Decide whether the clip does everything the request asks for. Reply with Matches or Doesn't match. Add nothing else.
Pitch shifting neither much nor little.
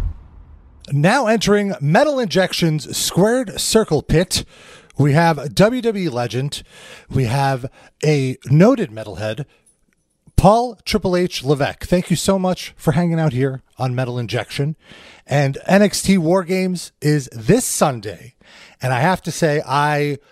Doesn't match